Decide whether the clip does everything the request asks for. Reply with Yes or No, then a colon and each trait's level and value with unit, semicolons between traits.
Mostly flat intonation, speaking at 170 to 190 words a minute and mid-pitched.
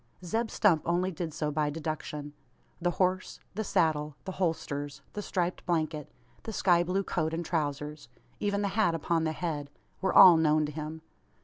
No: average, 3.3 semitones; average, 175 wpm; medium, 165 Hz